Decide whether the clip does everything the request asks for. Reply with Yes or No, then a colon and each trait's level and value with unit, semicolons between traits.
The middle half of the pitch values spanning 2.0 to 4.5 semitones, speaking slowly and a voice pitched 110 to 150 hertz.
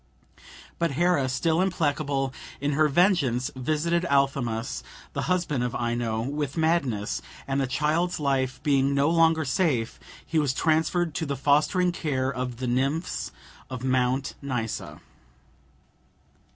Yes: average, 3.8 semitones; slow, 130 wpm; medium, 140 Hz